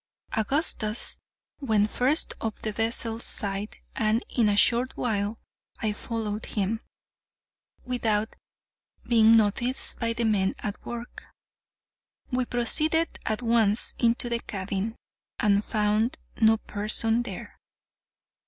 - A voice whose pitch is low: No, high, 225 Hz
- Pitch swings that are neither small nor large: No, narrow, 2.1 semitones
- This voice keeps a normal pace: No, slow, 115 wpm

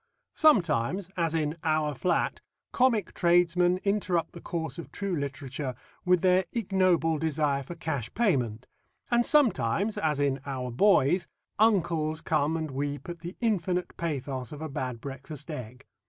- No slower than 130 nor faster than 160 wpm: Yes, average, 145 wpm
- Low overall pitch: No, medium, 160 Hz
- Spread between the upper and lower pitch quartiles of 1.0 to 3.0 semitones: No, average, 4.5 semitones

